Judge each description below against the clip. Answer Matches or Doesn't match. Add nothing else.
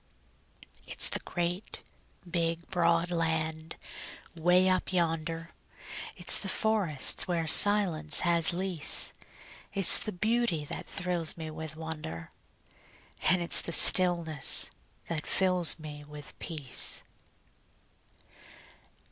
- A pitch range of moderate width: Doesn't match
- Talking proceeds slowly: Matches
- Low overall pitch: Doesn't match